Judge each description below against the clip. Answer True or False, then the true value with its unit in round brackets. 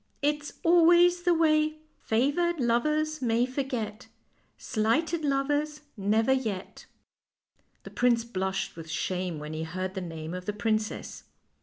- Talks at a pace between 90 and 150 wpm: True (145 wpm)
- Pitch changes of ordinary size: False (8.0 semitones)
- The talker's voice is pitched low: False (240 Hz)